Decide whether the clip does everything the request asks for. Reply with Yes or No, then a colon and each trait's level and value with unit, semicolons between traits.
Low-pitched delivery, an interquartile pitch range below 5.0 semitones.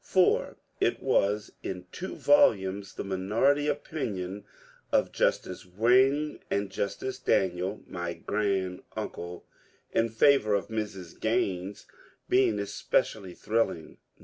Yes: low, 100 Hz; average, 4.3 semitones